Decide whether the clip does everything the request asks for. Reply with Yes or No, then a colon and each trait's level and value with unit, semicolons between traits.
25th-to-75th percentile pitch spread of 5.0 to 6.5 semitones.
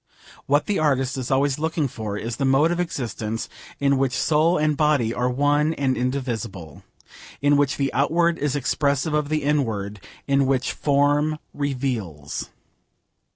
No: average, 3.1 semitones